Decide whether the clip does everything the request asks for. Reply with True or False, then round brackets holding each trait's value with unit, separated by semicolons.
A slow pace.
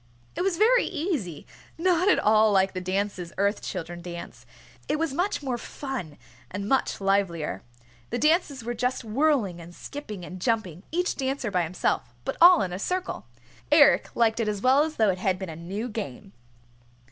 False (180 wpm)